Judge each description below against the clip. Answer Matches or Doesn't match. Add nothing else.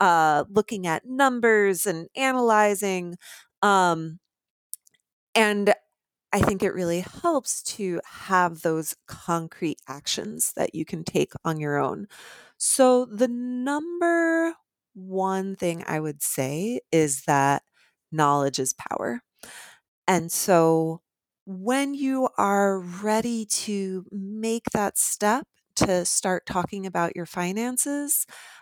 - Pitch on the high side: Matches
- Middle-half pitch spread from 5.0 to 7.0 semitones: Matches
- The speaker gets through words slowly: Matches